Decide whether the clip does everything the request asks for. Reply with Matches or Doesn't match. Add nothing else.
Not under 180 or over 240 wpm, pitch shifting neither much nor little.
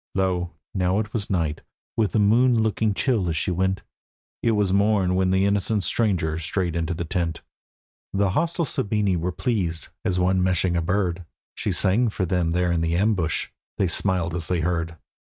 Matches